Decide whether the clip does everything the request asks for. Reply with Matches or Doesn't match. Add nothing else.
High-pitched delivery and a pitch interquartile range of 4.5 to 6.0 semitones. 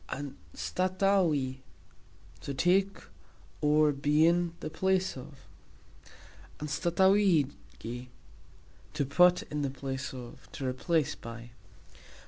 Doesn't match